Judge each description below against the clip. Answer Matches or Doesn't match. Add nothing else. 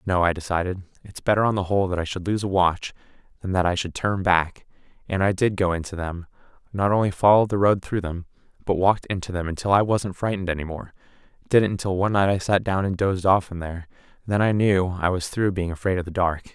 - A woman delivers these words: Doesn't match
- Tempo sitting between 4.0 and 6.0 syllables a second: Doesn't match